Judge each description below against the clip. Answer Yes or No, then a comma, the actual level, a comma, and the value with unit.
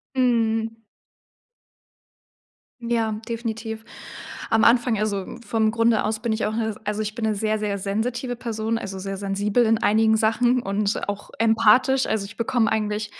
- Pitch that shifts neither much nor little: No, narrow, 1.6 semitones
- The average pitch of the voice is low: No, high, 220 Hz